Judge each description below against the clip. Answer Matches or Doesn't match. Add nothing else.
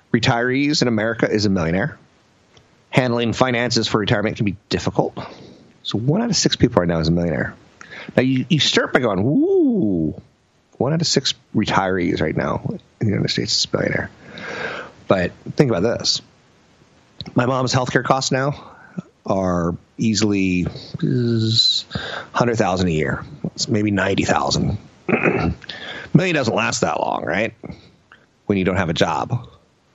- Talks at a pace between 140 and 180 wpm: Matches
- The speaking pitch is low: Matches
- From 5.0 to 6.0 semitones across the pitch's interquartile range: Matches